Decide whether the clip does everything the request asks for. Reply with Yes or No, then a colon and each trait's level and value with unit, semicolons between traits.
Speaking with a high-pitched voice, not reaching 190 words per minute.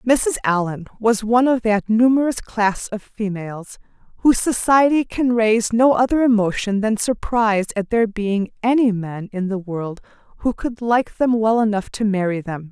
Yes: high, 220 Hz; average, 170 wpm